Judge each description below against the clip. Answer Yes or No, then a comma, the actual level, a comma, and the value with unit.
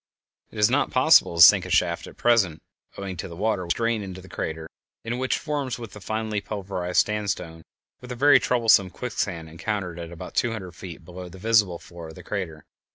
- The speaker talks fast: Yes, fast, 210 wpm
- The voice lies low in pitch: Yes, low, 100 Hz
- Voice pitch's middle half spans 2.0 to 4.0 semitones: No, average, 4.6 semitones